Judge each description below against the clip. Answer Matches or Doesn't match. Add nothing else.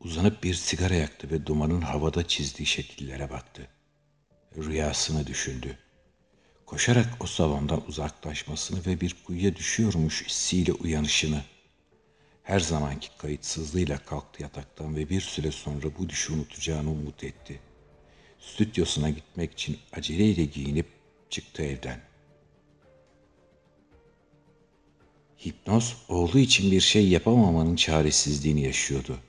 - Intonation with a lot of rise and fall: Doesn't match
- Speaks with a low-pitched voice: Matches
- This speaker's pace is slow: Doesn't match